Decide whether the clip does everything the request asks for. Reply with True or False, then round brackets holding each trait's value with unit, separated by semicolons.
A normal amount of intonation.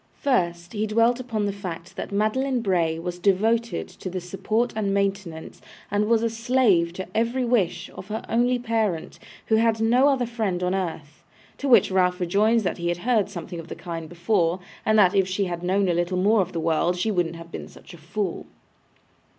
True (4.4 semitones)